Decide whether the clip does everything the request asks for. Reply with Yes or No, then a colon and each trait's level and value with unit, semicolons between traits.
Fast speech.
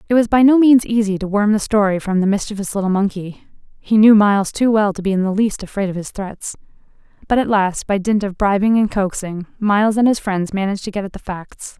Yes: fast, 245 wpm